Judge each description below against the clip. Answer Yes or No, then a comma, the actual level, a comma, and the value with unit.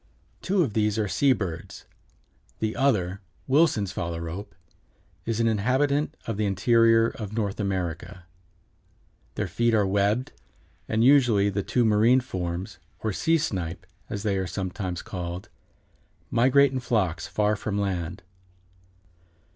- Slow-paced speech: Yes, slow, 130 wpm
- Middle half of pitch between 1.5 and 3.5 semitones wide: No, average, 3.9 semitones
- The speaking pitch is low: Yes, low, 105 Hz